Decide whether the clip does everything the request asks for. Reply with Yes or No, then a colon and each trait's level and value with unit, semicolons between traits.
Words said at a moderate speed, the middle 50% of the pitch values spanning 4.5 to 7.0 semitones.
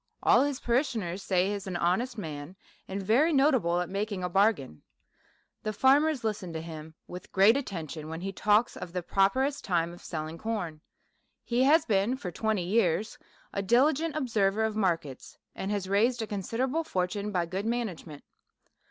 Yes: average, 175 wpm; average, 5.0 semitones